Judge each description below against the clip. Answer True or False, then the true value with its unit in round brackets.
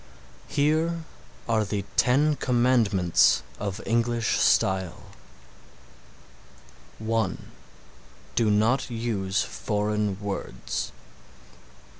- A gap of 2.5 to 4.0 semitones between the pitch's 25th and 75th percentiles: True (3.4 semitones)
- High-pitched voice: False (110 Hz)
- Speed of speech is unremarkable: False (70 wpm)